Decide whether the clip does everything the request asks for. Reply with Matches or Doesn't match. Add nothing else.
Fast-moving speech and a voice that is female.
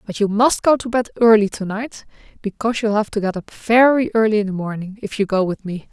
Matches